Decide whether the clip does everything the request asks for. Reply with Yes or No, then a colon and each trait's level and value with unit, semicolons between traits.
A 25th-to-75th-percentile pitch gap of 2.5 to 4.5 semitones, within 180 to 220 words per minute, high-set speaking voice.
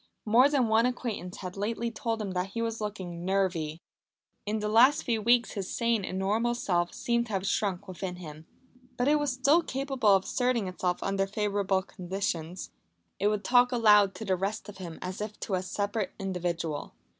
Yes: average, 3.9 semitones; average, 190 wpm; high, 205 Hz